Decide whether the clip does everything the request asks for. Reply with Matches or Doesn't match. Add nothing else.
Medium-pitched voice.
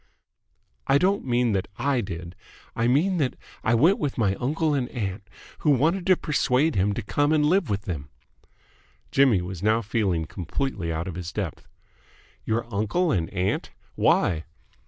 Doesn't match